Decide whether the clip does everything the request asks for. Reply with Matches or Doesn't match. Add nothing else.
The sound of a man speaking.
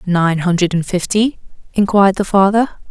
Doesn't match